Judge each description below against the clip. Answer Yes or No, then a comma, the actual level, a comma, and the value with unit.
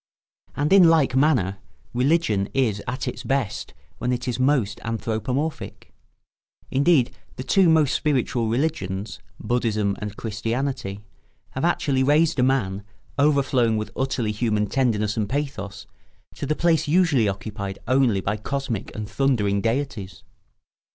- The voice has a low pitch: Yes, low, 125 Hz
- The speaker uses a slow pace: Yes, slow, 130 wpm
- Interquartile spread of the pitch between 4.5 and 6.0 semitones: Yes, average, 4.8 semitones